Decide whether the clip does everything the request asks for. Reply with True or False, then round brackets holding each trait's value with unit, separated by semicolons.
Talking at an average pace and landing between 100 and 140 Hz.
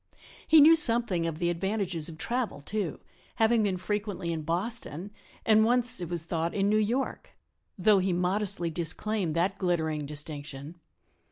False (155 wpm; 185 Hz)